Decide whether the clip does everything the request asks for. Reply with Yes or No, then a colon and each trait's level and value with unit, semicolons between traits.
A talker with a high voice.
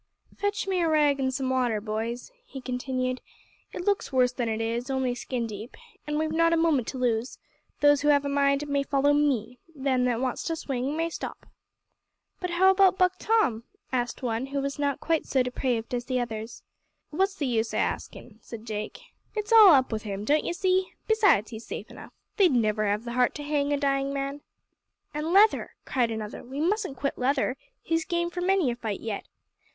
Yes: very high, 275 Hz